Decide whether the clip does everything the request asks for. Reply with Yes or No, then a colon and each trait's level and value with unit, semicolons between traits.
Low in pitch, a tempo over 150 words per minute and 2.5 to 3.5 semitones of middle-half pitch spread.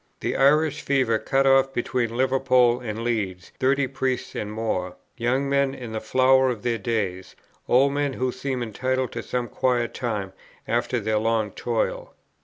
Yes: low, 125 Hz; average, 165 wpm; average, 2.9 semitones